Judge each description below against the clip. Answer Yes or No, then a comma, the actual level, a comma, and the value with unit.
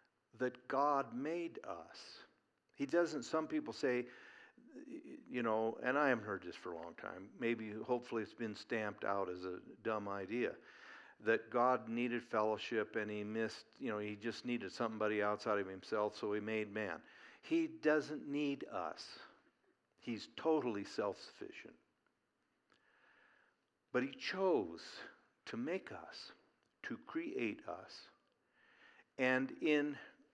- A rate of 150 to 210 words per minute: No, slow, 135 wpm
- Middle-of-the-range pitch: No, low, 120 Hz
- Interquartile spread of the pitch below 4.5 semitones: No, wide, 5.6 semitones